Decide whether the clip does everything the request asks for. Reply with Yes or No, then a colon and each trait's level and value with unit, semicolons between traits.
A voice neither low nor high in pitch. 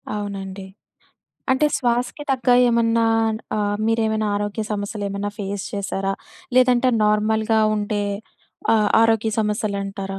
No: high, 210 Hz